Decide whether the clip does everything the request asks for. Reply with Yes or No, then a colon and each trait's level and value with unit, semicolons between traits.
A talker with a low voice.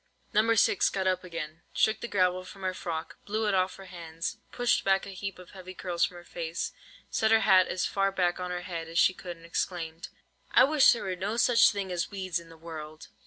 No: medium, 185 Hz